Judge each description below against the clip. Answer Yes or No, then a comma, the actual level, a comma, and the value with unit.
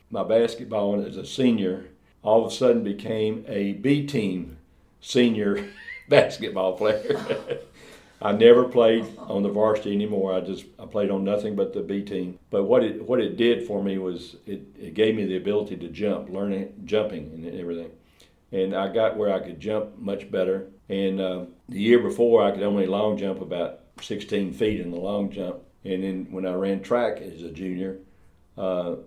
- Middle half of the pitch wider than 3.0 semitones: No, narrow, 2.5 semitones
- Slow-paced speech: No, average, 190 wpm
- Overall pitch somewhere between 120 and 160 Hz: No, low, 100 Hz